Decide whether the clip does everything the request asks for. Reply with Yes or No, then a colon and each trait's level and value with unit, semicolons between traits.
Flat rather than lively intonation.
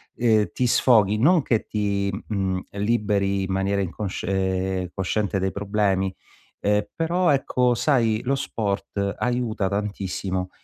No: average, 3.1 semitones